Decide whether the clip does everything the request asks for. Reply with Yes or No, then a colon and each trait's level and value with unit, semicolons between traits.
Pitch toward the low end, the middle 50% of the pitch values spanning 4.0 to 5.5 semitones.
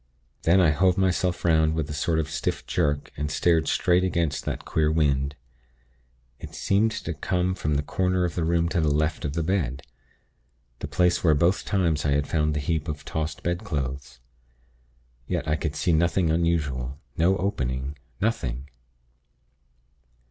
No: very low, 80 Hz; average, 3.2 semitones